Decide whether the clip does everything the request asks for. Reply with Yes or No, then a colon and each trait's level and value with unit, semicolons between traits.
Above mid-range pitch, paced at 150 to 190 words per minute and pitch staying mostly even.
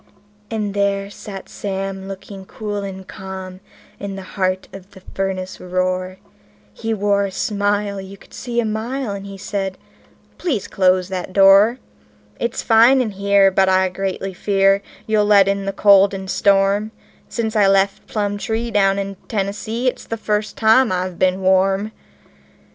Yes: high, 195 Hz; average, 160 wpm; narrow, 1.6 semitones